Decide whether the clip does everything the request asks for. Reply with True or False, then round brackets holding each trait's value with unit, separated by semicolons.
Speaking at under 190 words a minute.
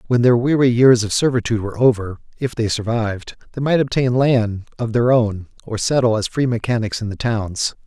False (200 wpm)